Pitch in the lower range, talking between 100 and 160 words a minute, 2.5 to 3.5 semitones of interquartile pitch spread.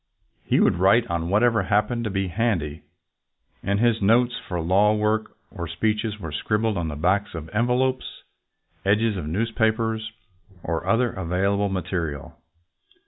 No: low, 105 Hz; average, 140 wpm; average, 4.2 semitones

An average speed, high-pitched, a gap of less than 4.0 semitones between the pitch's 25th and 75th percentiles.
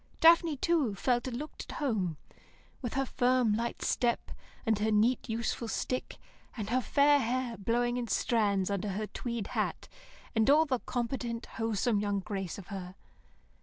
Yes: average, 165 wpm; high, 235 Hz; average, 3.5 semitones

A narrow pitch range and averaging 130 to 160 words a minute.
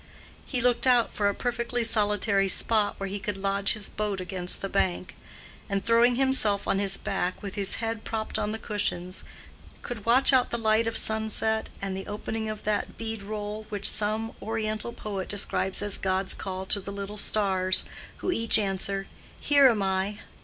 No: narrow, 2.3 semitones; average, 180 wpm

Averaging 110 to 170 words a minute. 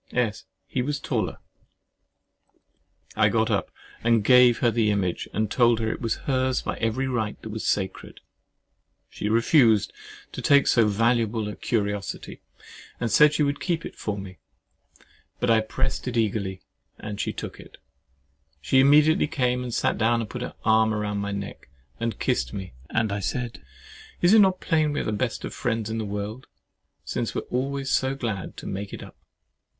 No: average, 185 wpm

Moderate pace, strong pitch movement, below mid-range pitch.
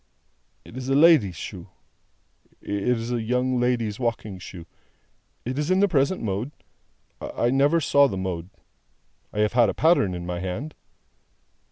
Yes: average, 160 wpm; wide, 5.8 semitones; low, 120 Hz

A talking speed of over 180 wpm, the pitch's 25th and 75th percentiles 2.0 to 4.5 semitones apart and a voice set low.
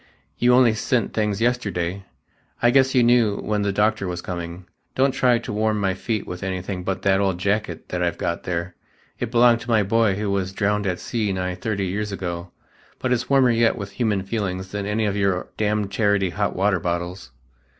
Yes: average, 200 wpm; average, 3.3 semitones; low, 100 Hz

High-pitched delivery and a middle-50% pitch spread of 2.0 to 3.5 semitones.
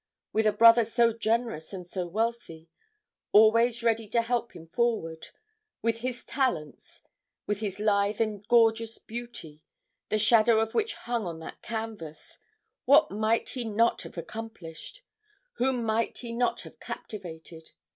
Yes: high, 225 Hz; average, 2.7 semitones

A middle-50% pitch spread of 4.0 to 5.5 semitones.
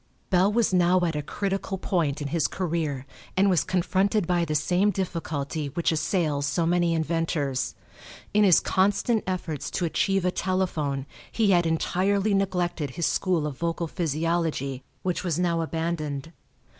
No: average, 3.3 semitones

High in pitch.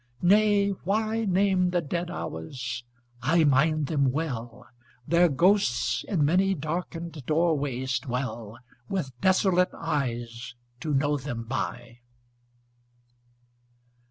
No: medium, 155 Hz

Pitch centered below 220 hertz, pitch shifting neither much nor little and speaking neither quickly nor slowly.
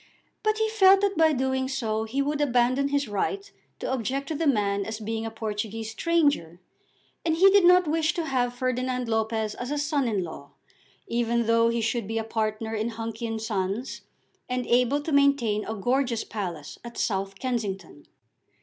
No: high, 235 Hz; average, 4.2 semitones; average, 185 wpm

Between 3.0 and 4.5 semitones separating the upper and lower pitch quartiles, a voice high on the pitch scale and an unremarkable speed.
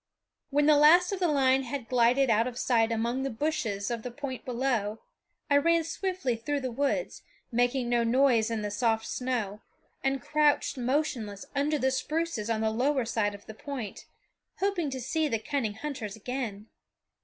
Yes: average, 4.1 semitones; very high, 255 Hz; average, 180 wpm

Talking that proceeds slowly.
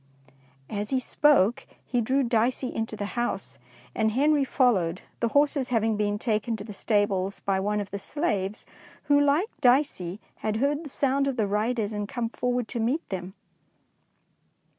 No: average, 170 wpm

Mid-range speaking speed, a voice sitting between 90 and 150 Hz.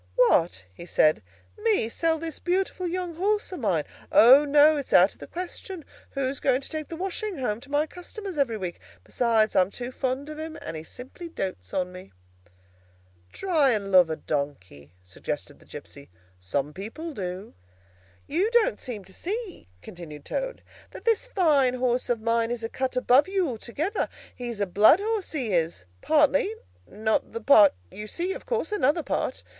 No: average, 175 wpm; very high, 260 Hz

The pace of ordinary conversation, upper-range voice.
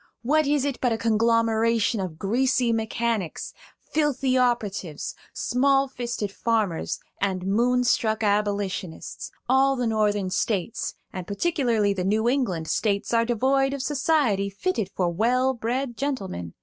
No: slow, 130 wpm; high, 230 Hz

